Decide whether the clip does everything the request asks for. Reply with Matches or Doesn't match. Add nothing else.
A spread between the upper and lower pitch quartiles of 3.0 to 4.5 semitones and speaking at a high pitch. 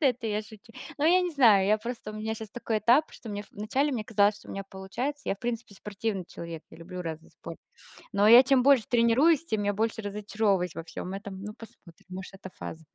Matches